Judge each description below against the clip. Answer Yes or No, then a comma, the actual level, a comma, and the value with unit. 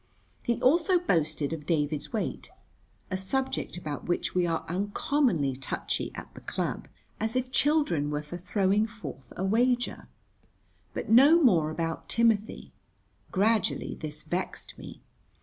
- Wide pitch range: Yes, wide, 7.2 semitones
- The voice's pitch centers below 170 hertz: No, high, 190 Hz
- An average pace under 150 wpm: Yes, average, 140 wpm